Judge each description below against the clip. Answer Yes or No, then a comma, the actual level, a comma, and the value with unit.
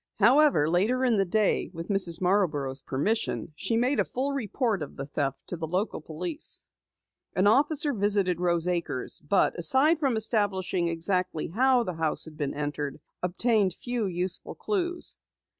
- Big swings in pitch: Yes, wide, 6.1 semitones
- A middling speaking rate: Yes, average, 155 wpm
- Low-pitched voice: No, high, 190 Hz